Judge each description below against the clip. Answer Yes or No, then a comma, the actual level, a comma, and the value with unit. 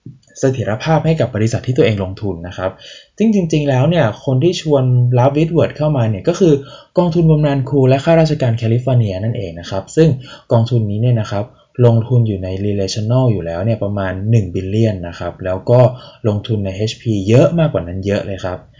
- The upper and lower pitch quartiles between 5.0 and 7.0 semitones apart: Yes, wide, 5.6 semitones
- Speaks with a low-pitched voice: Yes, low, 120 Hz